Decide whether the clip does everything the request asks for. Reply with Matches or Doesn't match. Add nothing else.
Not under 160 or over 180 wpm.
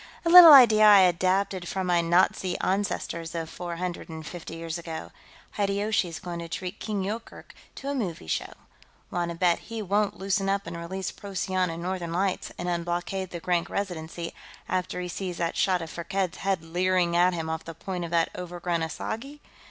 Doesn't match